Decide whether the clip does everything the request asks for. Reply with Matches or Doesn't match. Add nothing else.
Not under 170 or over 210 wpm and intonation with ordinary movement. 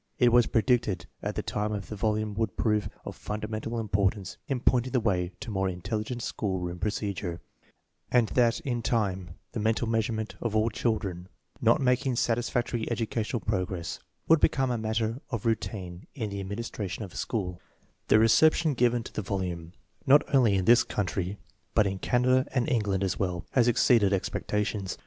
Matches